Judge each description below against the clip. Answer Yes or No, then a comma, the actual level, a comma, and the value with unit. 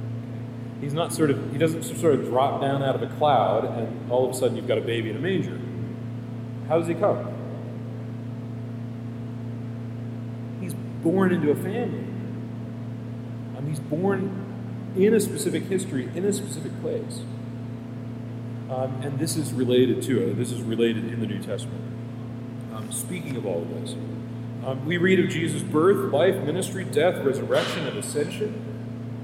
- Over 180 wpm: No, average, 160 wpm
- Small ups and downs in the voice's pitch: Yes, narrow, 1.4 semitones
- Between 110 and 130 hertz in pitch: Yes, low, 120 Hz